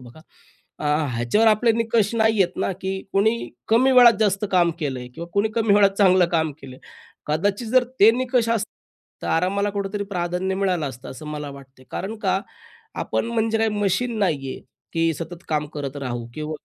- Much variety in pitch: Yes, wide, 6.2 semitones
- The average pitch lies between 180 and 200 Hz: Yes, high, 190 Hz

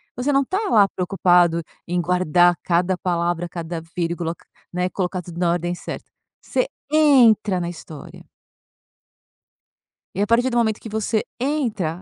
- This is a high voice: No, medium, 180 Hz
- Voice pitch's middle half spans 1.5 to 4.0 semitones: No, average, 4.5 semitones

